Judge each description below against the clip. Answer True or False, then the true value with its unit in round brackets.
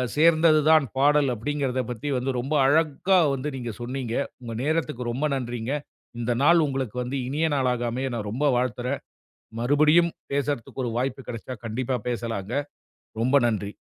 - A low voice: True (130 Hz)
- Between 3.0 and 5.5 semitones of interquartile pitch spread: True (3.4 semitones)